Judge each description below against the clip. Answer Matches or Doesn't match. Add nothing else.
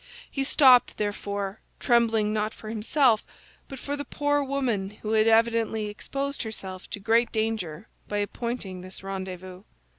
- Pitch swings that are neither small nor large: Matches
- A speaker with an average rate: Matches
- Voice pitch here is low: Doesn't match